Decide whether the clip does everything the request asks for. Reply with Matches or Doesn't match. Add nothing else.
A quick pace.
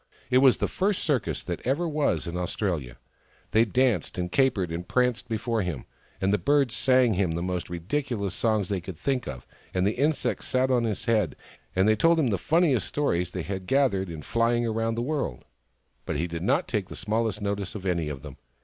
Matches